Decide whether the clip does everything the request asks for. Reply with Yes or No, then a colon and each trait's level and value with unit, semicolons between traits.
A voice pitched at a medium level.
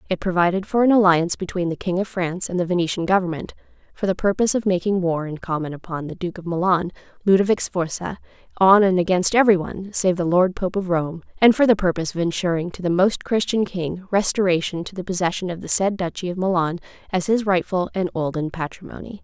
Yes: medium, 180 Hz